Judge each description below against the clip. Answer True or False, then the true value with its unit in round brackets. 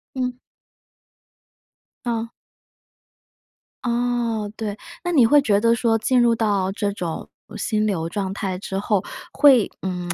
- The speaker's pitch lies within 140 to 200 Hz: False (220 Hz)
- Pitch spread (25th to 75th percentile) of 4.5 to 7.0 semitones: False (3.2 semitones)